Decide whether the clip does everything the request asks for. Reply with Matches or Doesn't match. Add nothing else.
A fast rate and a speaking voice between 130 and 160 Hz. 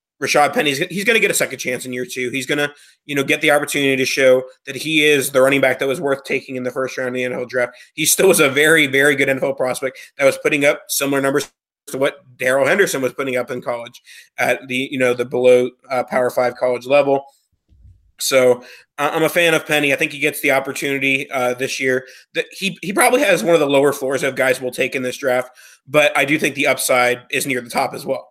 Matches